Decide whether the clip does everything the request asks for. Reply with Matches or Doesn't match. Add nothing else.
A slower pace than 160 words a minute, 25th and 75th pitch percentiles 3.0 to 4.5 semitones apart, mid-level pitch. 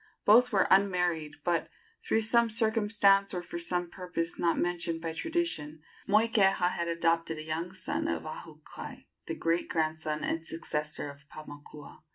Matches